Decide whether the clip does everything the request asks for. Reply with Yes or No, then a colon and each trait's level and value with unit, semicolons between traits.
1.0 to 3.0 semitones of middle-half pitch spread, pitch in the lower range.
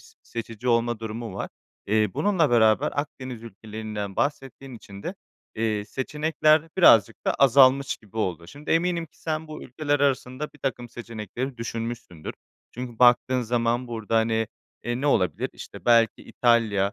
No: average, 3.7 semitones; low, 120 Hz